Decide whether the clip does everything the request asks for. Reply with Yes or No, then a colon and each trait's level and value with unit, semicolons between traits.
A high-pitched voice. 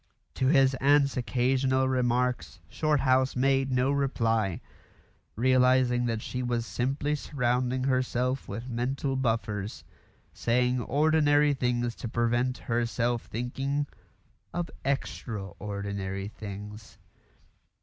No: low, 125 Hz